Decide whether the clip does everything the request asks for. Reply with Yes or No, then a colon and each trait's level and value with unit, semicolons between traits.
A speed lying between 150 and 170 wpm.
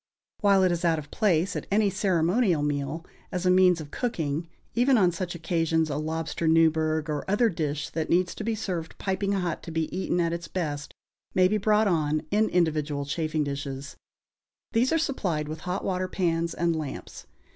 No: average, 185 wpm